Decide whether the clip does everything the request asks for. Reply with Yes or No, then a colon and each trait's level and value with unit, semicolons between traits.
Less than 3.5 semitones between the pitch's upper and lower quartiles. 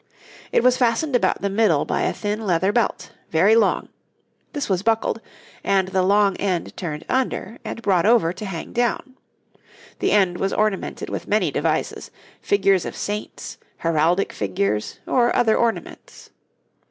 No: average, 4.2 semitones